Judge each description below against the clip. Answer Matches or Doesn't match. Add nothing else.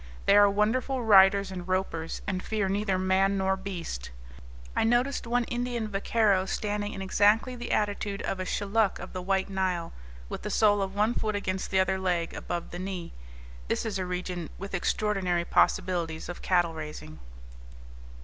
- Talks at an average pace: Matches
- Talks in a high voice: Matches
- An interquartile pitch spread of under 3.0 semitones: Matches